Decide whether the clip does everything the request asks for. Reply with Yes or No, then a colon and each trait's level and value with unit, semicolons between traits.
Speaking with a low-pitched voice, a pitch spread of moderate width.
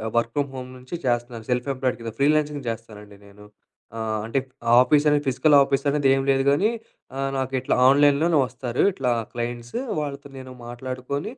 Yes: low, 130 Hz; average, 3.0 semitones